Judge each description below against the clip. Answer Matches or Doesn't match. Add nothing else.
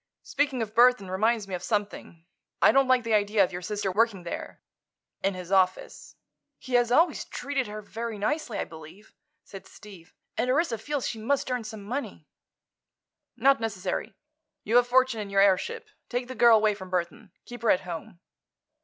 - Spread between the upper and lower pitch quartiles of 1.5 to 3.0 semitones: Doesn't match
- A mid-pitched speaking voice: Doesn't match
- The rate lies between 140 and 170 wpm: Doesn't match